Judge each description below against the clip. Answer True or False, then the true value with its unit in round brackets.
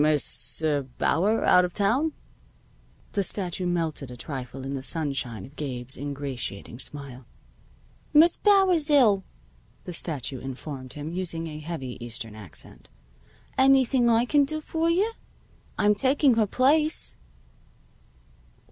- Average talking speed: False (130 wpm)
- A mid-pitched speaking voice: True (165 Hz)